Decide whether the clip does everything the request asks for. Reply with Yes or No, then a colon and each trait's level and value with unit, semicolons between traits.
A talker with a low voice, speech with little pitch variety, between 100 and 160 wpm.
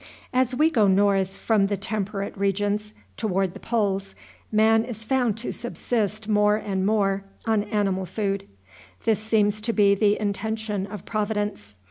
No: high, 210 Hz; narrow, 1.9 semitones; average, 150 wpm